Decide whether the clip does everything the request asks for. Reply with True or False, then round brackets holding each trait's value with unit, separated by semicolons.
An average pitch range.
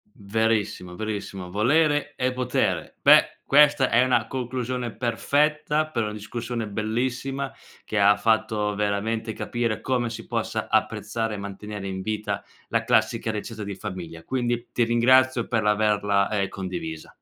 True (3.4 semitones)